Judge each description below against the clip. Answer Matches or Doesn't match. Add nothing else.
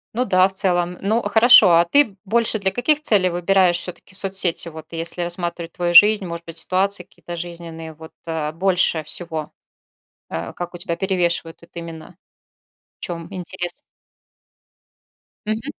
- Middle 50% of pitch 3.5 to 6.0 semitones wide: Doesn't match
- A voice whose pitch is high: Doesn't match